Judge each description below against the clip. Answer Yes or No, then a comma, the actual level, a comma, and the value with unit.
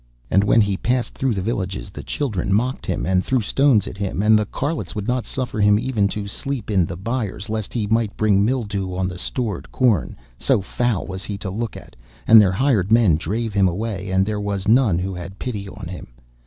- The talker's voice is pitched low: Yes, low, 105 Hz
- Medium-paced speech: No, fast, 220 wpm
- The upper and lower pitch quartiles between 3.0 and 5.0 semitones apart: Yes, average, 3.4 semitones